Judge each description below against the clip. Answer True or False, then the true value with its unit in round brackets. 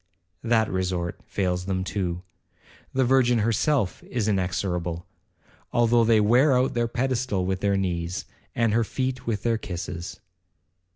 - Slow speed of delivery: True (130 wpm)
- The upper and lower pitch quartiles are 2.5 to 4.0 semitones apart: False (4.6 semitones)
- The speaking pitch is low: True (105 Hz)